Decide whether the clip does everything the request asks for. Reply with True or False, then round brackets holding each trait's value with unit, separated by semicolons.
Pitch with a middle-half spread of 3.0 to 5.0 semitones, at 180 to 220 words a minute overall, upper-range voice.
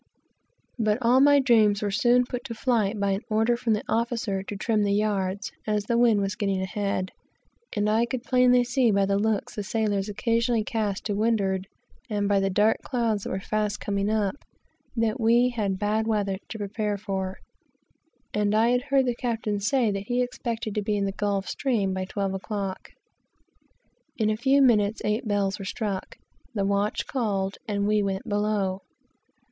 False (2.6 semitones; 185 wpm; 210 Hz)